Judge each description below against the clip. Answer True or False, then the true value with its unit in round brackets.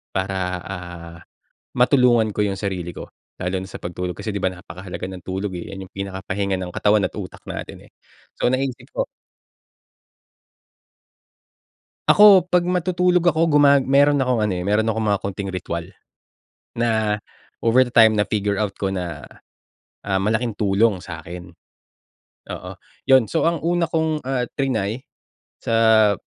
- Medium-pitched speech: False (105 Hz)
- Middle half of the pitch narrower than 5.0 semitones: False (5.6 semitones)